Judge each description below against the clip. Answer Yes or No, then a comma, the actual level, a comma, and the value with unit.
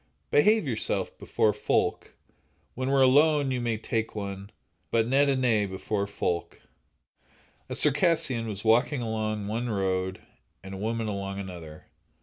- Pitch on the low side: Yes, low, 110 Hz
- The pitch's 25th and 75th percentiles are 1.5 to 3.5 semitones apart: No, average, 4.7 semitones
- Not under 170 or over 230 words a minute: No, average, 140 wpm